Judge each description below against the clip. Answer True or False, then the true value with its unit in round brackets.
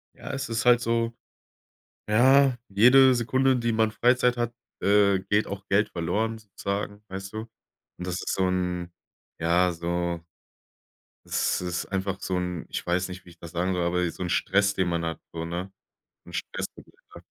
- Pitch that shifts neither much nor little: True (4.4 semitones)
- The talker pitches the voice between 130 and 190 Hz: False (95 Hz)